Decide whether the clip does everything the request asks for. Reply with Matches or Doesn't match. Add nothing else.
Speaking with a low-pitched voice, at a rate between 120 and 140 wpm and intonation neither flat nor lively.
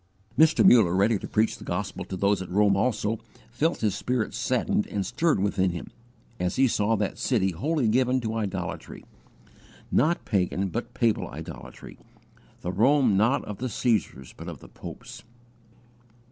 Doesn't match